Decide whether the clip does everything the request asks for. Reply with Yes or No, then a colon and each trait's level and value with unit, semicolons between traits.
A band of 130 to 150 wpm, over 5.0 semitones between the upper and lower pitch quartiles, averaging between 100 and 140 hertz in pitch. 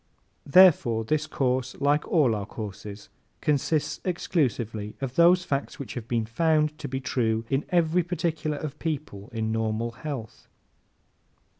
Yes: average, 140 wpm; wide, 5.5 semitones; low, 135 Hz